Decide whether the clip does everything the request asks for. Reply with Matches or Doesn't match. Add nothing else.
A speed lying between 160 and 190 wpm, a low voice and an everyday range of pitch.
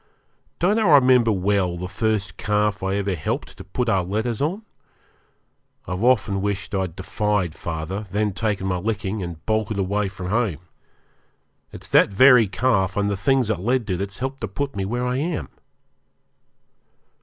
Matches